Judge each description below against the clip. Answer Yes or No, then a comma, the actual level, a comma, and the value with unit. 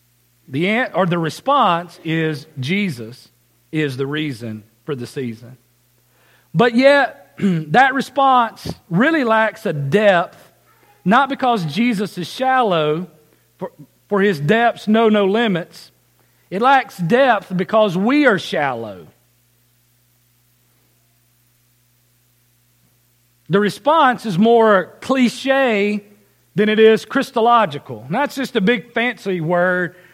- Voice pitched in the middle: Yes, medium, 180 Hz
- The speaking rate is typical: No, slow, 110 wpm